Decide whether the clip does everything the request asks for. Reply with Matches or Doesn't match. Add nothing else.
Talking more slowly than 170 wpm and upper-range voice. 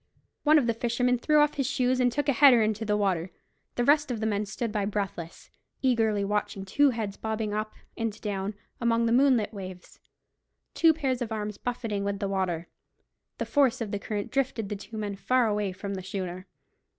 Doesn't match